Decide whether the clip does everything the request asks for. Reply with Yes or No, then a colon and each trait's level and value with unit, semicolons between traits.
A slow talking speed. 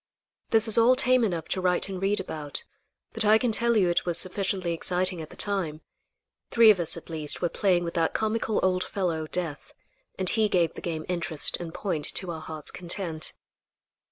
No: average, 200 wpm